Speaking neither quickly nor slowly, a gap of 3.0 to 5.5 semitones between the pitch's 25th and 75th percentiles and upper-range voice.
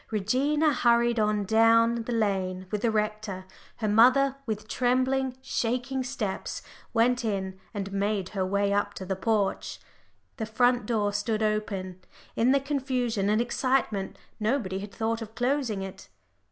Yes: average, 150 wpm; average, 3.4 semitones; high, 220 Hz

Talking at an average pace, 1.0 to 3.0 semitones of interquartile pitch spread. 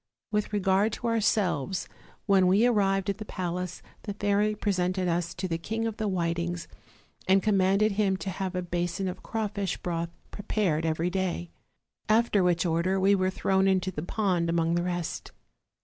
Yes: average, 170 wpm; average, 2.7 semitones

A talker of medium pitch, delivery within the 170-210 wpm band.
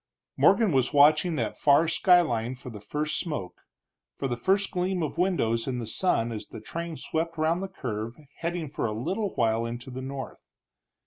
Yes: medium, 145 Hz; average, 185 wpm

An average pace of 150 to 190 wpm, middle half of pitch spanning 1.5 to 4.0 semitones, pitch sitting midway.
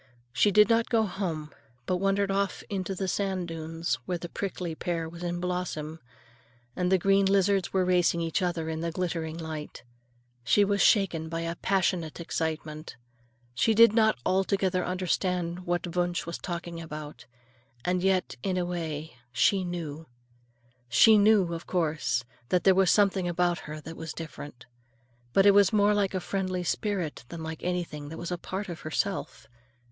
Yes: average, 170 wpm; average, 2.9 semitones; medium, 175 Hz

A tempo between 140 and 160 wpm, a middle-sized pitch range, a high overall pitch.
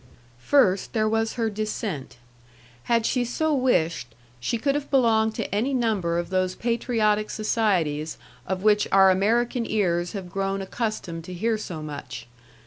Yes: average, 150 wpm; average, 4.2 semitones; high, 210 Hz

